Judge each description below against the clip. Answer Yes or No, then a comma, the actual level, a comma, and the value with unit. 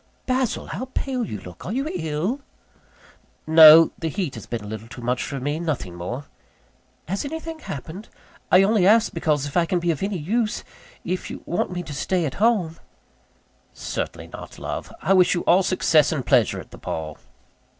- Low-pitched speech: No, medium, 170 Hz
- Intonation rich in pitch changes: Yes, wide, 5.8 semitones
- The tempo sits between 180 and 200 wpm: Yes, average, 190 wpm